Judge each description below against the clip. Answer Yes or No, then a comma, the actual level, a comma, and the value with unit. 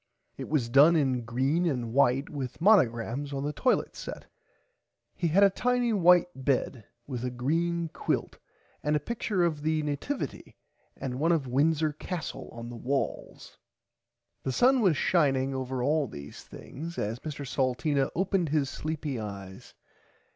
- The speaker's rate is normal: Yes, average, 155 wpm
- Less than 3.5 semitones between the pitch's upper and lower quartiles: No, average, 4.6 semitones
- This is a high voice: No, medium, 145 Hz